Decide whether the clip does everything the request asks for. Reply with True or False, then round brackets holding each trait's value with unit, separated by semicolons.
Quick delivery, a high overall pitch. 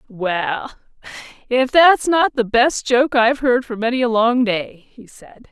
False (175 wpm; 240 Hz)